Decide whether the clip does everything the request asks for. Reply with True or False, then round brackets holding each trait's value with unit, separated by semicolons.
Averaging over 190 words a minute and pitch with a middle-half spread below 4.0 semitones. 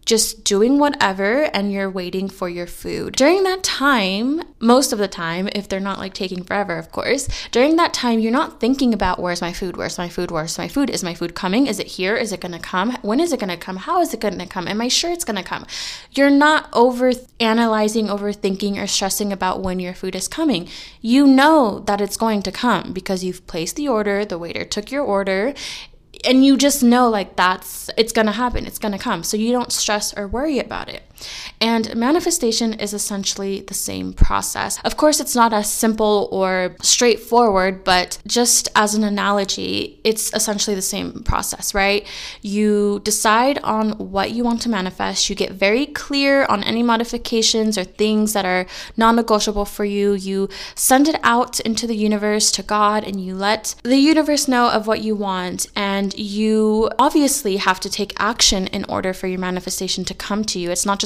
True (200 wpm; 3.6 semitones)